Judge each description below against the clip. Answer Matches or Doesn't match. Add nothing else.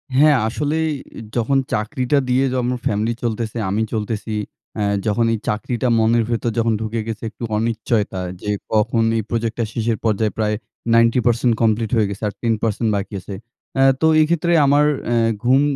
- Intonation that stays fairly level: Matches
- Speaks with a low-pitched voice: Matches